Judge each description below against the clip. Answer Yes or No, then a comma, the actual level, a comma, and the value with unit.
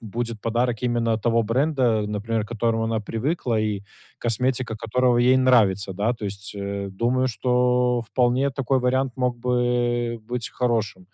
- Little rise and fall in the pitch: Yes, narrow, 2.1 semitones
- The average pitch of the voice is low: Yes, low, 120 Hz